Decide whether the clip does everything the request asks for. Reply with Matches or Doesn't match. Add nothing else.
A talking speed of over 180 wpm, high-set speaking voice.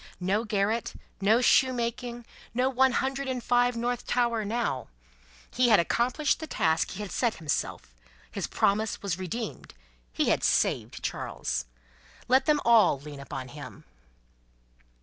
Doesn't match